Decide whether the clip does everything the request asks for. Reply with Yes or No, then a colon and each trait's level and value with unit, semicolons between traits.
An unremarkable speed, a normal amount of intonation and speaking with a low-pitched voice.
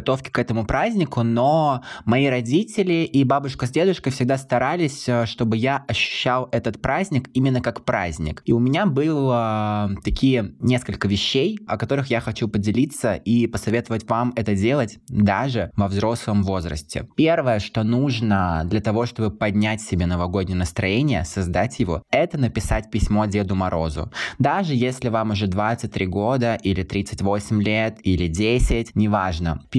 Yes: average, 145 wpm; average, 3.9 semitones; low, 115 Hz